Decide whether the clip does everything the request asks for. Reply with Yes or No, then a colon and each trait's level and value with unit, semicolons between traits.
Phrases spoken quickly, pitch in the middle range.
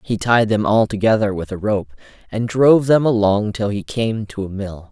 No: fast, 220 wpm; low, 105 Hz